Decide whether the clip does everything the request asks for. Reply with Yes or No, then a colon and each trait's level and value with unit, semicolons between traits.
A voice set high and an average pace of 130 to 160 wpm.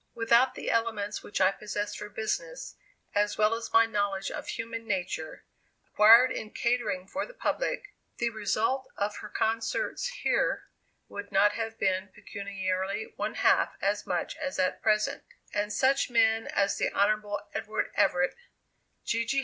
Yes: high, 215 Hz; average, 155 wpm